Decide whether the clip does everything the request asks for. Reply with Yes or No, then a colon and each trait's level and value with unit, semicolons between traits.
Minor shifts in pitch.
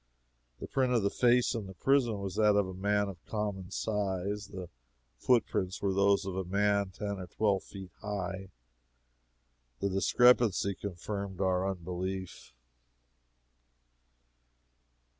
Yes: narrow, 1.7 semitones